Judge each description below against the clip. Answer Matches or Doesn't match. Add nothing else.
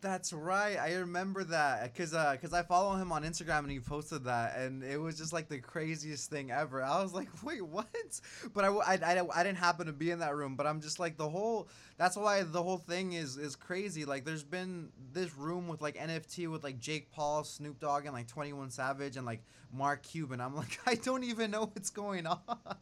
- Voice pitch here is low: Doesn't match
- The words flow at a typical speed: Doesn't match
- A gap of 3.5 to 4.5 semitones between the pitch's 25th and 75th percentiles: Matches